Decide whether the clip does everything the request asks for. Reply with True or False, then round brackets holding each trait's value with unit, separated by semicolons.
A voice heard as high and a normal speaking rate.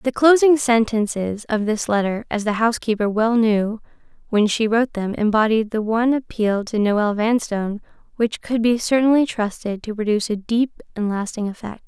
True (220 Hz; 160 wpm)